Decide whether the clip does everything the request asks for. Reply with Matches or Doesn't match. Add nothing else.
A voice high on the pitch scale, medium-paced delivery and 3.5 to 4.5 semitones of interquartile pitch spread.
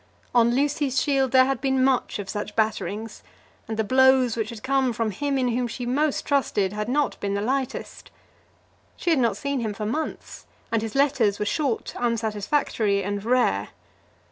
Matches